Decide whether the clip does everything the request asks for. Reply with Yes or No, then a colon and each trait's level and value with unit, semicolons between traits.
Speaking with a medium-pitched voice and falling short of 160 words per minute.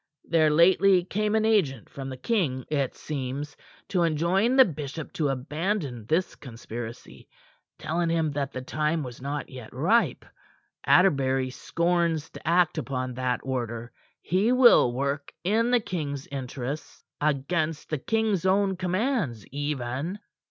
Yes: medium, 155 Hz; average, 140 wpm